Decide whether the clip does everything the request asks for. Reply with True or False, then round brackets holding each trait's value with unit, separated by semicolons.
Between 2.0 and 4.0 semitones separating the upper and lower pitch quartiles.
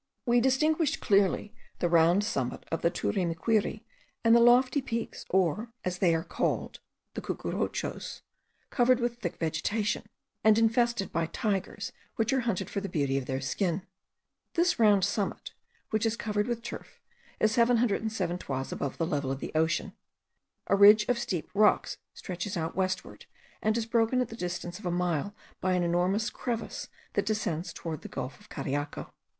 False (4.9 semitones)